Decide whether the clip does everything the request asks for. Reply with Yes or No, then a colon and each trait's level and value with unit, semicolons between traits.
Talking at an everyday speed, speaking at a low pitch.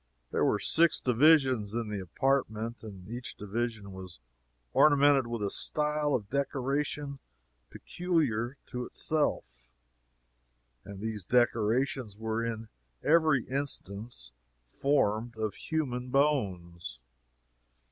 No: slow, 105 wpm; low, 120 Hz